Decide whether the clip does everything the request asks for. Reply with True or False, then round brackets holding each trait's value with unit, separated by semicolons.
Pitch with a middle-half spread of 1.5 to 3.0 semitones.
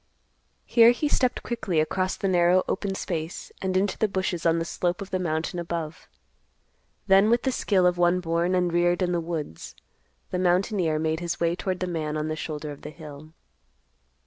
True (2.5 semitones)